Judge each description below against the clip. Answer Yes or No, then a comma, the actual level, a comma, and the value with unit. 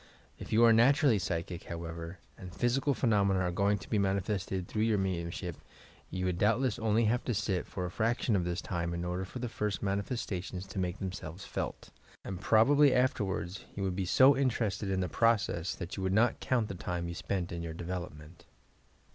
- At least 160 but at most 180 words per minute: No, average, 200 wpm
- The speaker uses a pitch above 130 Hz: No, very low, 95 Hz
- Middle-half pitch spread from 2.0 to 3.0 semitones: No, average, 4.1 semitones